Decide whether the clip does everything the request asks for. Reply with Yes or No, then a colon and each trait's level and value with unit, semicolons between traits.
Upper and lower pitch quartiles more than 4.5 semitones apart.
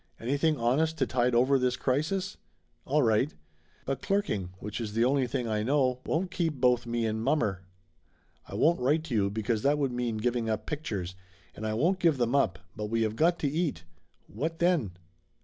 Yes: average, 5.3 semitones